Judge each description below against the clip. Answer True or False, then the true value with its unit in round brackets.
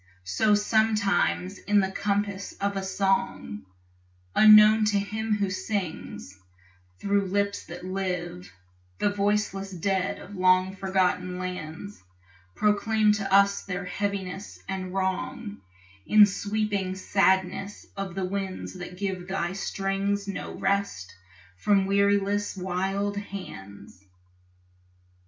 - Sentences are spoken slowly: True (110 wpm)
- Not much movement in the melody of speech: True (1.6 semitones)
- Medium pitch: False (195 Hz)